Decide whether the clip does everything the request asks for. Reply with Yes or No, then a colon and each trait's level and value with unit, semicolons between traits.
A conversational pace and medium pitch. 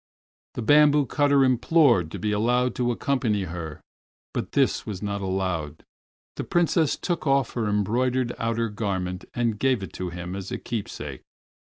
No: average, 160 wpm; low, 115 Hz